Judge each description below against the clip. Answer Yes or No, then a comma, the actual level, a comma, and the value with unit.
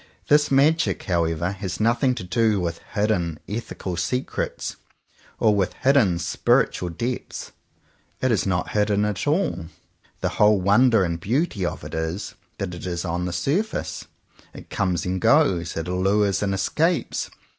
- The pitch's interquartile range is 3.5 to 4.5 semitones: No, average, 5.2 semitones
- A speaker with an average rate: Yes, average, 150 wpm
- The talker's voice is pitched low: Yes, low, 100 Hz